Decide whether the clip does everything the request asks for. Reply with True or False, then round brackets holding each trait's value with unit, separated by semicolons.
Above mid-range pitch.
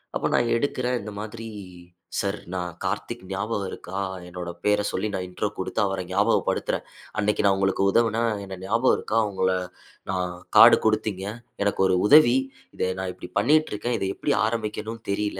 False (105 Hz)